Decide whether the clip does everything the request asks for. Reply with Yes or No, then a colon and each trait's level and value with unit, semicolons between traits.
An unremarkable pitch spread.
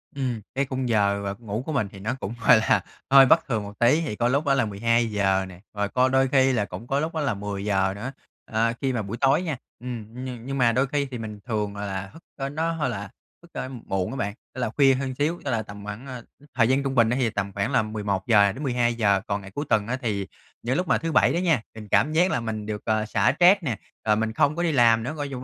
Yes: average, 4.6 semitones